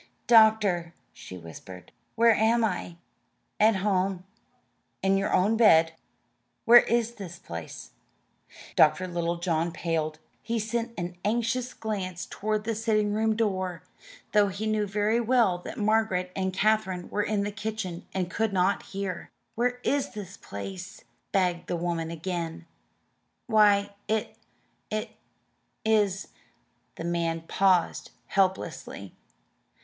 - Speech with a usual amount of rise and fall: Yes, average, 3.8 semitones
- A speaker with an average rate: No, slow, 125 wpm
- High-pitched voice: Yes, high, 195 Hz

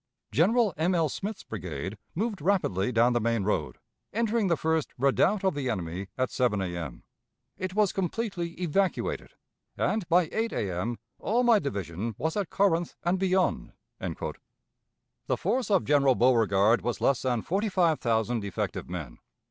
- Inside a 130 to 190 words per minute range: Yes, average, 155 wpm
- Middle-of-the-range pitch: Yes, medium, 150 Hz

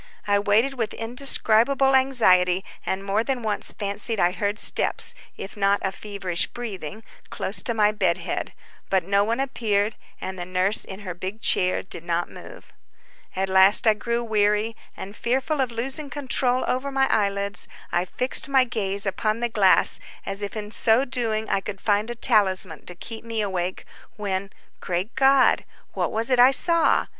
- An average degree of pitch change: Yes, average, 3.6 semitones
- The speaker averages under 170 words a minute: No, average, 175 wpm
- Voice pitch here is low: No, high, 210 Hz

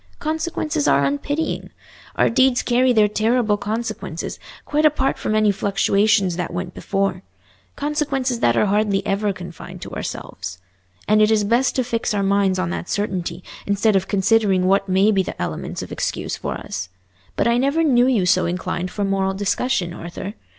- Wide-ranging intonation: No, average, 4.3 semitones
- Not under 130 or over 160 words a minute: No, average, 170 wpm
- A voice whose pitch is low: No, high, 205 Hz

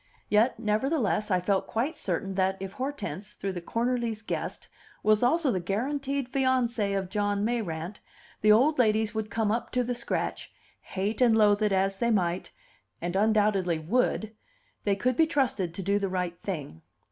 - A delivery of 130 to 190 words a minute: Yes, average, 170 wpm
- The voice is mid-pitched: No, high, 210 Hz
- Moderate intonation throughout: Yes, average, 3.9 semitones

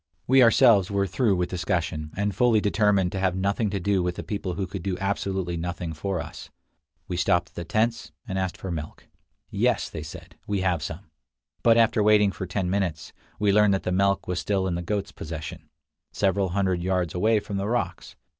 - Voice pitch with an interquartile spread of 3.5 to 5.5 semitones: No, narrow, 2.5 semitones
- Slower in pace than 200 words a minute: No, fast, 205 wpm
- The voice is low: Yes, very low, 95 Hz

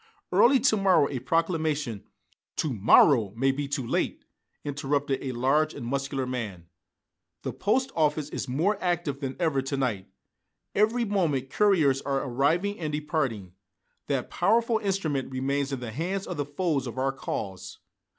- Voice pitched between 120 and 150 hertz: Yes, medium, 140 Hz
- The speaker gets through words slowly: No, average, 160 wpm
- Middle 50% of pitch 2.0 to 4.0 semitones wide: No, average, 4.8 semitones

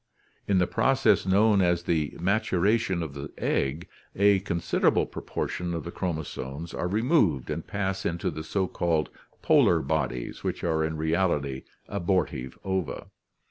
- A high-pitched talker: No, very low, 85 Hz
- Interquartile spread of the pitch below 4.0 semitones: Yes, average, 3.5 semitones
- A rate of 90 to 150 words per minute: Yes, average, 140 wpm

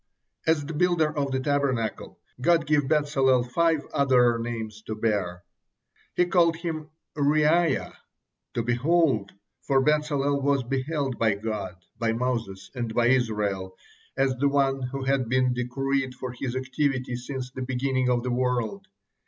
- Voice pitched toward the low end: Yes, low, 130 Hz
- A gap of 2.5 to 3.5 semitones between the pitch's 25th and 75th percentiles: Yes, average, 3.1 semitones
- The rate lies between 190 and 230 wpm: No, average, 145 wpm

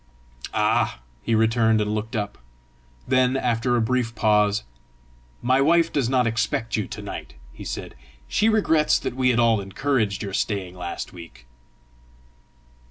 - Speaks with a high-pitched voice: No, low, 115 Hz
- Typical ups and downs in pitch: Yes, average, 3.6 semitones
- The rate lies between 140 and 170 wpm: Yes, average, 150 wpm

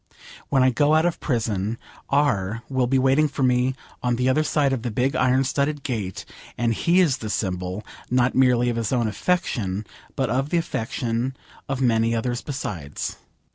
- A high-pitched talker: No, low, 125 Hz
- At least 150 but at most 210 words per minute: Yes, average, 180 wpm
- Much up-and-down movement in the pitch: No, average, 3.1 semitones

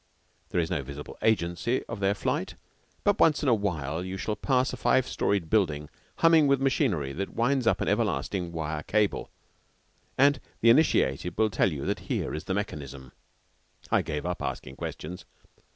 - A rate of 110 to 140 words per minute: No, average, 170 wpm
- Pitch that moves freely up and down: Yes, wide, 7.8 semitones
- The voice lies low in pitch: Yes, very low, 95 Hz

